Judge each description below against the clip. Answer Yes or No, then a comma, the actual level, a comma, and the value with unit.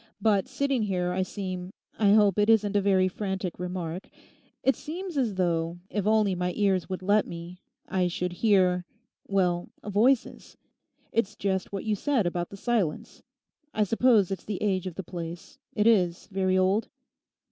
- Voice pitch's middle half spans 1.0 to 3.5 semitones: Yes, average, 2.9 semitones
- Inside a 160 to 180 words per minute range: Yes, average, 165 wpm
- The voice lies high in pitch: Yes, high, 195 Hz